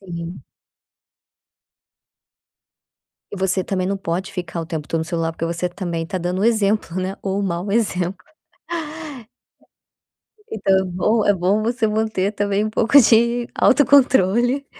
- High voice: Yes, high, 195 Hz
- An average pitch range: Yes, average, 3.7 semitones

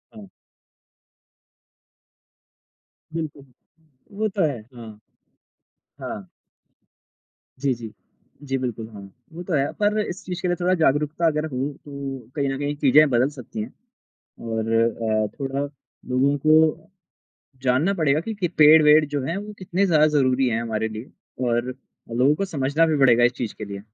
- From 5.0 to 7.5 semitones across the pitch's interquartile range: No, average, 4.6 semitones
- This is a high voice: No, medium, 140 Hz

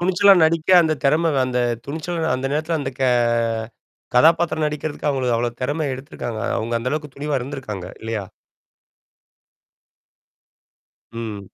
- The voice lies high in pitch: No, medium, 140 Hz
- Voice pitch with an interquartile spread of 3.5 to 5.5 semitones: Yes, average, 4.5 semitones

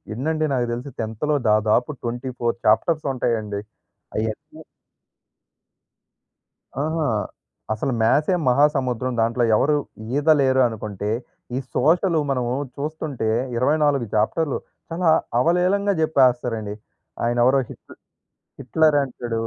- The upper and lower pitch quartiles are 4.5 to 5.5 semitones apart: Yes, average, 4.8 semitones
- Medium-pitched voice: No, low, 130 Hz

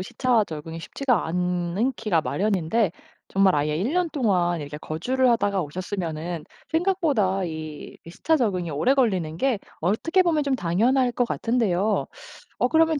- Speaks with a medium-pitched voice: No, high, 200 Hz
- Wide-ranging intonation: Yes, wide, 7.0 semitones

